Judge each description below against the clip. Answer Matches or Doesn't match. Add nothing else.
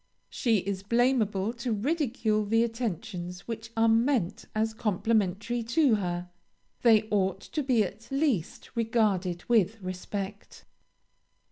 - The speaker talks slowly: Matches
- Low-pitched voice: Doesn't match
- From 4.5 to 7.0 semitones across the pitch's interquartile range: Doesn't match